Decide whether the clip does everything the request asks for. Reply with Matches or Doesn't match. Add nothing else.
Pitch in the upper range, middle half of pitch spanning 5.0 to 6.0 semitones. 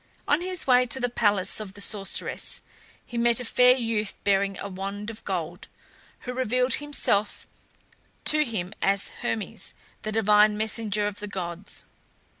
Doesn't match